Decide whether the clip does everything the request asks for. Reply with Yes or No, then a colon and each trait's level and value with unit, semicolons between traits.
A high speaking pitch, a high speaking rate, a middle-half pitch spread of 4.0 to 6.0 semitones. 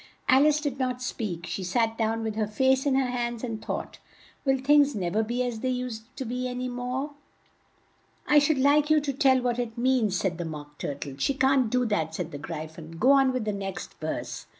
Yes: high, 245 Hz; fast, 230 wpm; average, 4.4 semitones